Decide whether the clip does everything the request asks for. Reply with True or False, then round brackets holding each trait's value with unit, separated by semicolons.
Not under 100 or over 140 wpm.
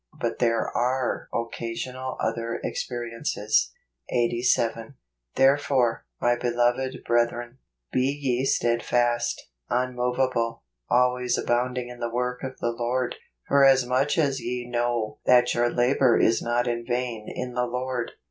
True (135 wpm)